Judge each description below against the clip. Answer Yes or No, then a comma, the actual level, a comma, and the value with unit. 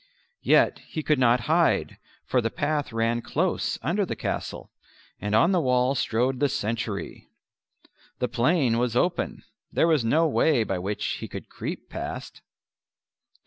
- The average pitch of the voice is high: No, low, 125 Hz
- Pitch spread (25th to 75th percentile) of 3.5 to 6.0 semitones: Yes, wide, 5.4 semitones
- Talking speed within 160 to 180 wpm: No, average, 150 wpm